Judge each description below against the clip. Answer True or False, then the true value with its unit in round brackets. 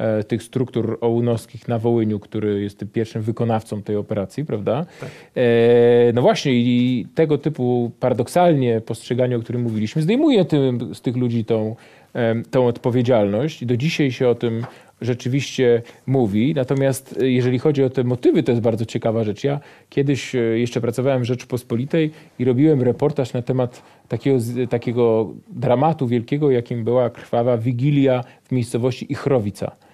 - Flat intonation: True (2.2 semitones)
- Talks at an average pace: True (145 wpm)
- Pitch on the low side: True (125 Hz)